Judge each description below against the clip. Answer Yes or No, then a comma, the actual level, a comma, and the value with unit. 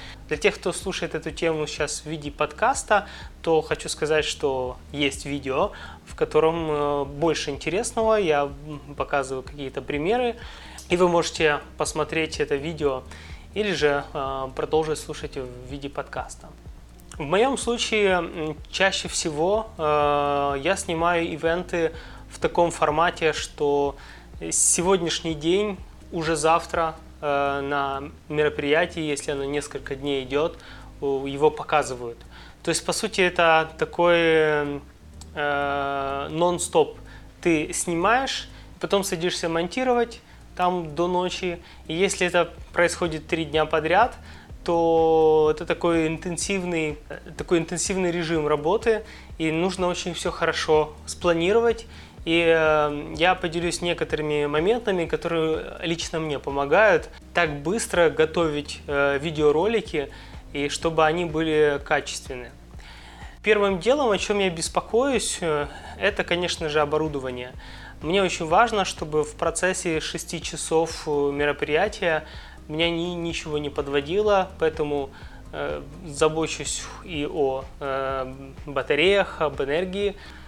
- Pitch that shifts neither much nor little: Yes, average, 3.2 semitones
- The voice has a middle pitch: Yes, medium, 160 Hz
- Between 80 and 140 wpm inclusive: Yes, slow, 110 wpm